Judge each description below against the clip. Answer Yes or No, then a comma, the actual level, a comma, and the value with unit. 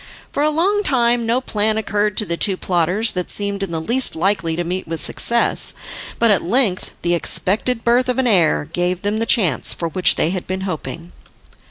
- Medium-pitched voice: No, high, 200 Hz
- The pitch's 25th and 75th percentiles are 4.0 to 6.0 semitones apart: Yes, average, 5.0 semitones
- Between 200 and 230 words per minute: Yes, fast, 205 wpm